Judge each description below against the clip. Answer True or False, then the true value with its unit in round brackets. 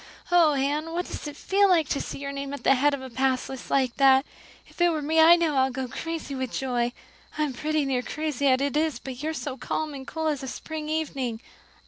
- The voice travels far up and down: False (3.0 semitones)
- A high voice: True (285 Hz)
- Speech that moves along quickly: True (250 wpm)